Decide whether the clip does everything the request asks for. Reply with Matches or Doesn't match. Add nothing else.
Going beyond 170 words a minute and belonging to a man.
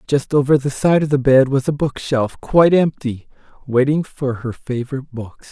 Matches